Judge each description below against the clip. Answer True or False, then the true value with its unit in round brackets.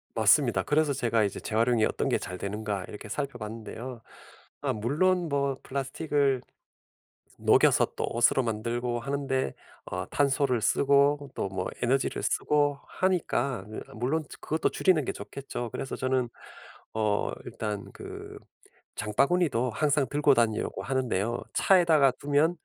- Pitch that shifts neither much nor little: True (4.3 semitones)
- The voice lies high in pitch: False (130 Hz)